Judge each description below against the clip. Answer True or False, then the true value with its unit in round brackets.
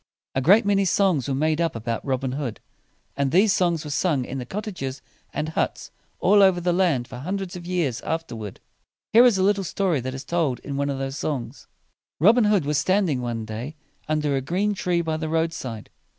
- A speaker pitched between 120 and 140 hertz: False (155 Hz)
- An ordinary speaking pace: False (220 wpm)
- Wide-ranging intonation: True (5.7 semitones)